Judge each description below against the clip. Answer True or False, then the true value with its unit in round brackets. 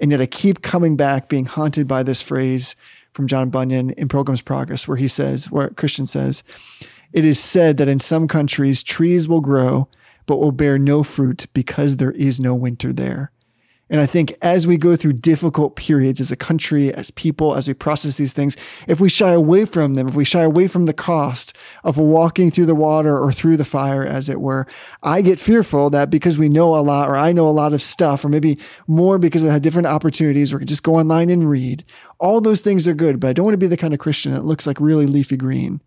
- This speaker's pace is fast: True (235 wpm)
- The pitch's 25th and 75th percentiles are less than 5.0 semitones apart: True (3.2 semitones)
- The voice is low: False (150 Hz)